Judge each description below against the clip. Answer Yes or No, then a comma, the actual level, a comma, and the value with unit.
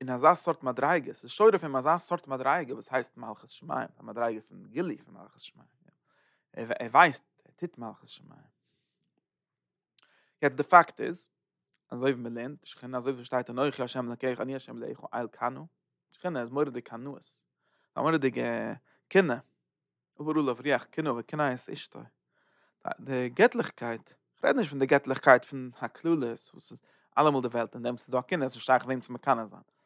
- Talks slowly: No, average, 185 wpm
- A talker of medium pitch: No, low, 130 Hz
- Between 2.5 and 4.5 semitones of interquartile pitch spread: Yes, average, 3.6 semitones